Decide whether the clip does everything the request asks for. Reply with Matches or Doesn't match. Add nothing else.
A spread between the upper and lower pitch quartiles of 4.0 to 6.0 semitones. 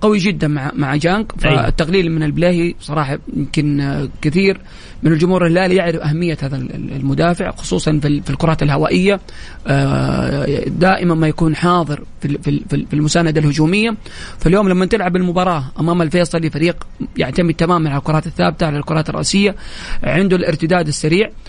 Doesn't match